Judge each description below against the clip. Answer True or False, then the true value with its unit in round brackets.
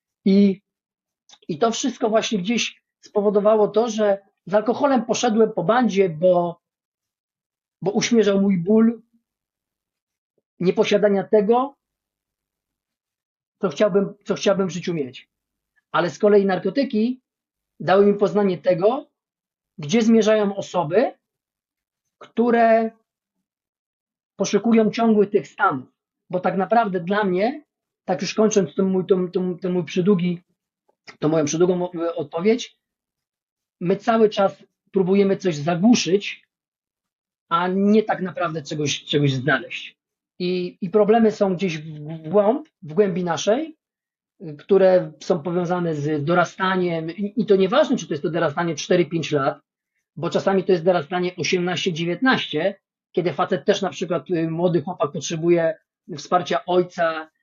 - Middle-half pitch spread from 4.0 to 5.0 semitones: False (3.3 semitones)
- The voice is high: True (195 Hz)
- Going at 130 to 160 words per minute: False (120 wpm)